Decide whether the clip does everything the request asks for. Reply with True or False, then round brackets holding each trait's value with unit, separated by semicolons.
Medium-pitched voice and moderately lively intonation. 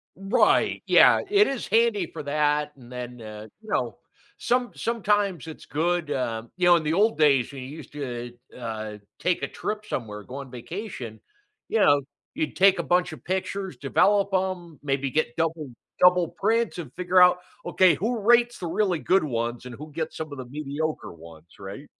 False (160 Hz; 6.8 semitones)